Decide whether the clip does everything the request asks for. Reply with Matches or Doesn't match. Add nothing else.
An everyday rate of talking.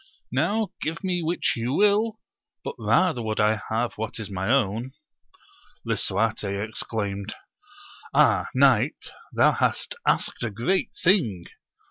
Doesn't match